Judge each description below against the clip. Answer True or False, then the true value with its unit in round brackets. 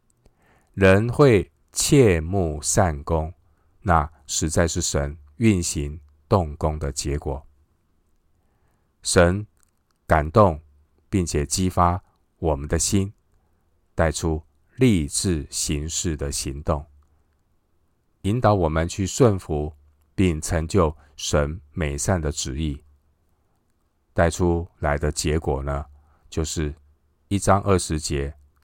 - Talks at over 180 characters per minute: False (140 characters per minute)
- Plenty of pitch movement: False (3.6 semitones)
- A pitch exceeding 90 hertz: False (80 Hz)